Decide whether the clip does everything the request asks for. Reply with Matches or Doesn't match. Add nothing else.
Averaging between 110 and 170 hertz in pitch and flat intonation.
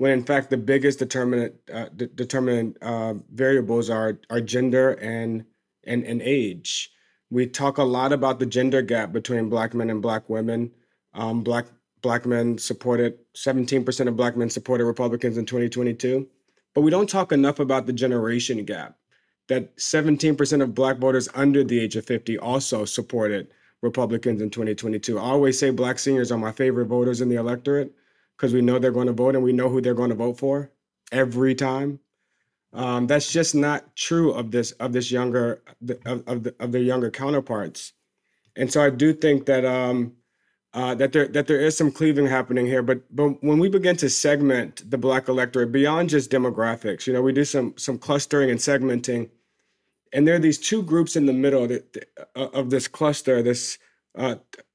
Matches